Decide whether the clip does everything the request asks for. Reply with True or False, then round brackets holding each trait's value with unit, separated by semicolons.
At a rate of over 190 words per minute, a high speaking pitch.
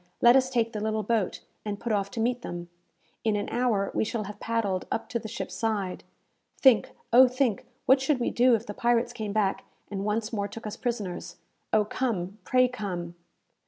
True (200 wpm; 220 Hz)